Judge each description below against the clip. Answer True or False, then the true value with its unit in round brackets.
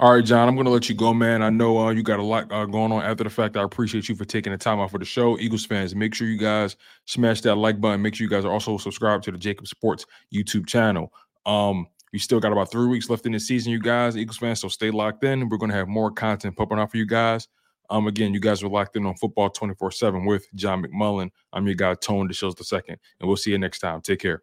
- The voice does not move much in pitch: True (2.0 semitones)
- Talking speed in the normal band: False (285 wpm)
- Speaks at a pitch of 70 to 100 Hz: False (110 Hz)